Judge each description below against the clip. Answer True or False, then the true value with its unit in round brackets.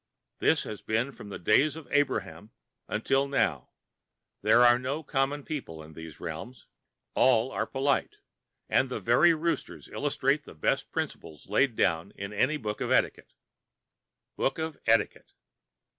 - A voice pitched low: True (125 Hz)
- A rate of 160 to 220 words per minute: False (145 wpm)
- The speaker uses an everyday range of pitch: False (5.7 semitones)